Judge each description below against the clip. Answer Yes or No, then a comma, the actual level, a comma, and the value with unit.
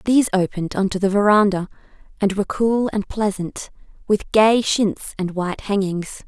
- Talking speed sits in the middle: Yes, average, 165 wpm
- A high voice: Yes, high, 200 Hz